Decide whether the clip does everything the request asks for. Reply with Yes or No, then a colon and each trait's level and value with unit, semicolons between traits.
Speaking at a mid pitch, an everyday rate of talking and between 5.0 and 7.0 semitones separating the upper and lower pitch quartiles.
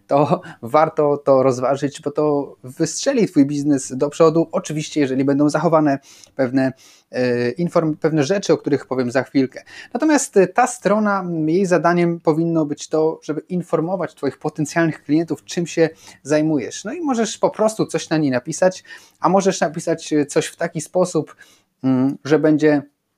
No: medium, 155 Hz; average, 150 wpm; average, 3.2 semitones